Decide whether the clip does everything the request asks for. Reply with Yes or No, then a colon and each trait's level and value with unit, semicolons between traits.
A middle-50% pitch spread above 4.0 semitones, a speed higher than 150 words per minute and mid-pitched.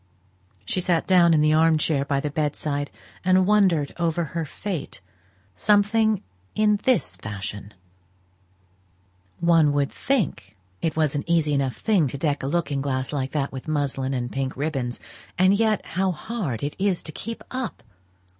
Yes: average, 5.1 semitones; average, 165 wpm; medium, 155 Hz